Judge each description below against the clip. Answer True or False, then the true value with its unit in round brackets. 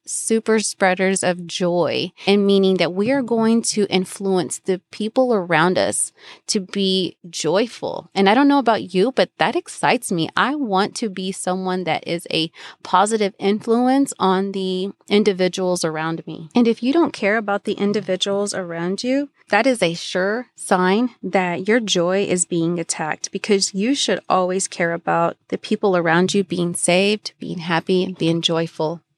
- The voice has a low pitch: False (190 Hz)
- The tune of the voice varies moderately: True (3.4 semitones)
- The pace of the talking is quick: False (170 wpm)